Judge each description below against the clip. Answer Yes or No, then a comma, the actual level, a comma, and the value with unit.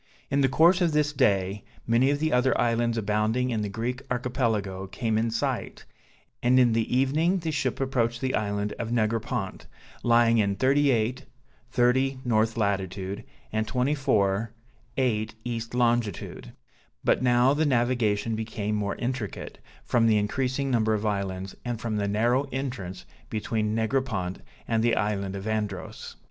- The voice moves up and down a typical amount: Yes, average, 3.3 semitones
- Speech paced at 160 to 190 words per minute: No, average, 150 wpm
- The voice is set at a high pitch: No, low, 115 Hz